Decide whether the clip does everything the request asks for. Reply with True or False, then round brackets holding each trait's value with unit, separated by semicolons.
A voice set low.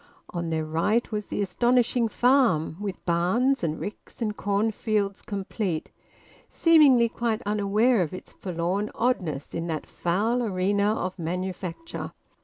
False (205 Hz)